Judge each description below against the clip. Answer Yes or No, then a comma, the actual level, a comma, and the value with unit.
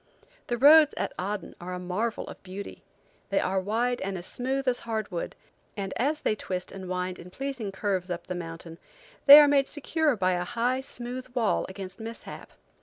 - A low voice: No, high, 205 Hz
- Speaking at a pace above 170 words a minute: Yes, average, 185 wpm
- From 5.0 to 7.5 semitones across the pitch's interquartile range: Yes, wide, 5.5 semitones